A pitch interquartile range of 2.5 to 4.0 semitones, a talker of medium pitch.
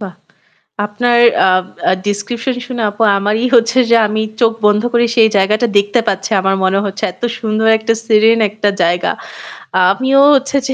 No: average, 2.8 semitones; high, 220 Hz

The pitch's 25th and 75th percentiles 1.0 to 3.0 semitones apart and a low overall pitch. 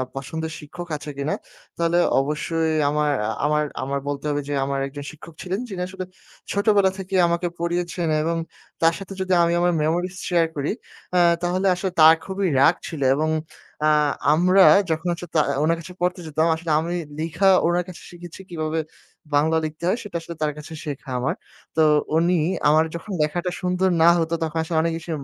No: narrow, 2.4 semitones; medium, 165 Hz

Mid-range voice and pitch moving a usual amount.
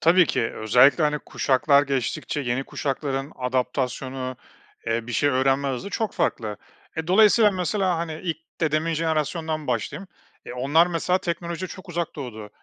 Yes: medium, 150 Hz; average, 4.7 semitones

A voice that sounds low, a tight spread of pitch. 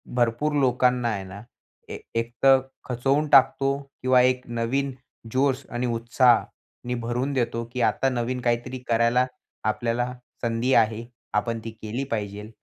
Yes: low, 120 Hz; narrow, 1.9 semitones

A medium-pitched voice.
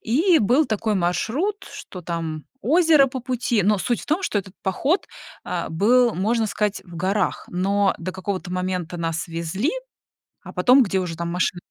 No: high, 200 Hz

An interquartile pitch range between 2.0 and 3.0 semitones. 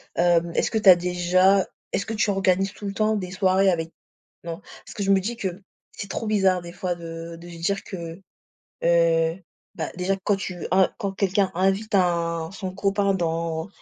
Yes: narrow, 2.5 semitones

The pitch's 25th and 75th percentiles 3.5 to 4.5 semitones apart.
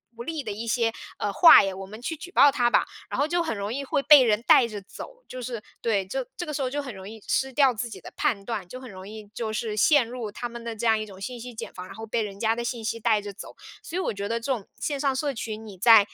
Yes: average, 3.8 semitones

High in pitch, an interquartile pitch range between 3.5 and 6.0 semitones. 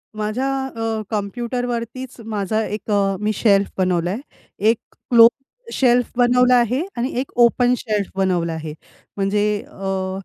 Yes: high, 220 Hz; average, 3.8 semitones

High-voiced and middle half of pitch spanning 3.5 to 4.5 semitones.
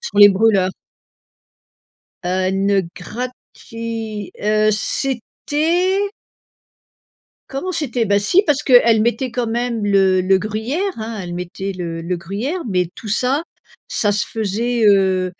Yes: high, 215 Hz; average, 4.2 semitones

